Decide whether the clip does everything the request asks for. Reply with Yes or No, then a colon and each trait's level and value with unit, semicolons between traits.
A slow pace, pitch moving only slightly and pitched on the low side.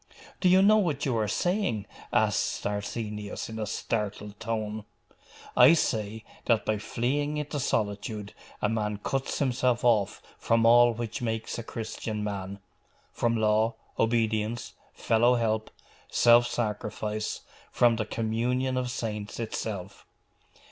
Yes: slow, 130 wpm; narrow, 2.2 semitones; low, 115 Hz